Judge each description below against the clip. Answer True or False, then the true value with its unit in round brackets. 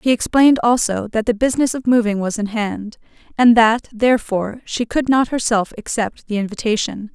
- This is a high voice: True (225 Hz)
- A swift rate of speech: False (175 wpm)